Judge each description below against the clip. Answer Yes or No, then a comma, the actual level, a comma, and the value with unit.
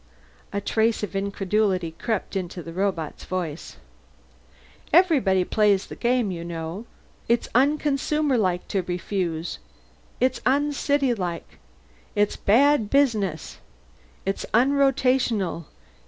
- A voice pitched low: No, high, 205 Hz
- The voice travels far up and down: Yes, wide, 6.0 semitones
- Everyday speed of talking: No, slow, 95 wpm